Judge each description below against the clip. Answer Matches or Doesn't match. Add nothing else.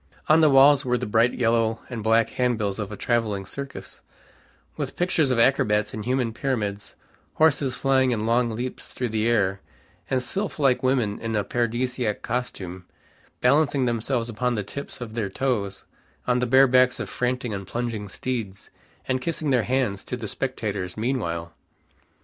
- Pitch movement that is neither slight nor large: Matches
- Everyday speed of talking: Matches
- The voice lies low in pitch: Matches